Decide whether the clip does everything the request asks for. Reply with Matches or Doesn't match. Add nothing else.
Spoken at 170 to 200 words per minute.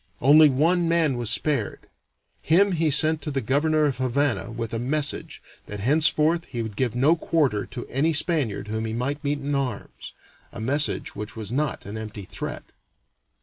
Matches